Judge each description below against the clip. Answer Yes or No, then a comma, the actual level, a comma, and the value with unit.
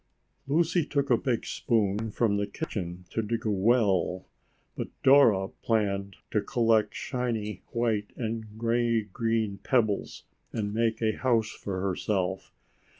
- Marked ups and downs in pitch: No, narrow, 2.6 semitones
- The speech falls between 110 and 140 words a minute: Yes, slow, 135 wpm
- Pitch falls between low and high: No, low, 110 Hz